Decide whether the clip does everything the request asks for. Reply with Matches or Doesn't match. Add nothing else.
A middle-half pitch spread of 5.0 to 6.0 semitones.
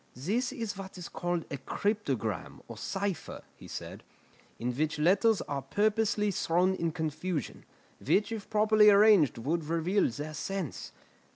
Matches